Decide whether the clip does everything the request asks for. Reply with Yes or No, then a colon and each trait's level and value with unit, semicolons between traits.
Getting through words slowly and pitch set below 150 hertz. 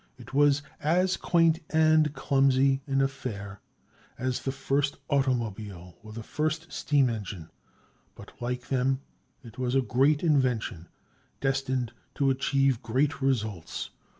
Yes: slow, 125 wpm; low, 135 Hz